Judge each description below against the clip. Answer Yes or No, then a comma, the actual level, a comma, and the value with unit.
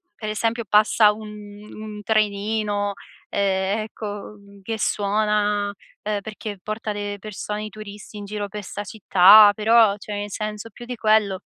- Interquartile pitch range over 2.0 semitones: No, narrow, 1.0 semitones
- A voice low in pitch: No, high, 210 Hz